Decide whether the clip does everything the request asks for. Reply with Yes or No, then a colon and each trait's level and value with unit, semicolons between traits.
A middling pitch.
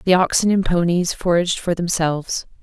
Yes: medium, 175 Hz